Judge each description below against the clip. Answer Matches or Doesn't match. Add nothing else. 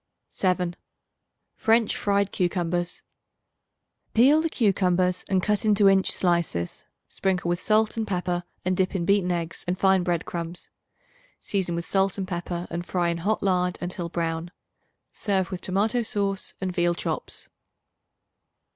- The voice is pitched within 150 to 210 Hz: Matches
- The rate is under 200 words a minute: Matches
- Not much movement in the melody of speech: Matches